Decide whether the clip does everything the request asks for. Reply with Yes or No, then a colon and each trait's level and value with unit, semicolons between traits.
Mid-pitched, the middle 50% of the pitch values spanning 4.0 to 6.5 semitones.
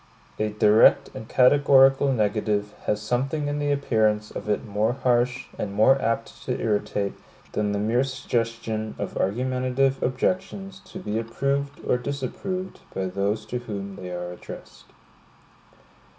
No: low, 115 Hz; average, 4.4 semitones